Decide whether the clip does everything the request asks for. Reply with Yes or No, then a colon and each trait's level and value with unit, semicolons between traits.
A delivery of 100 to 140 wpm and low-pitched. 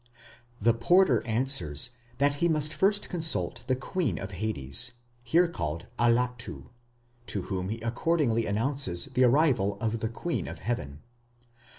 Yes: slow, 135 wpm; low, 120 Hz